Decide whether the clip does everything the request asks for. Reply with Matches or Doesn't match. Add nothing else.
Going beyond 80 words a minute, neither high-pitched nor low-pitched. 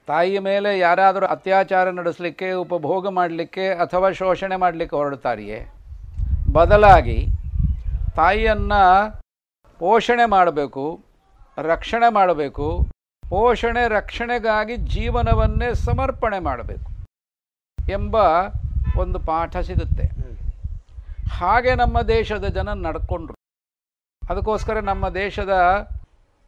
Doesn't match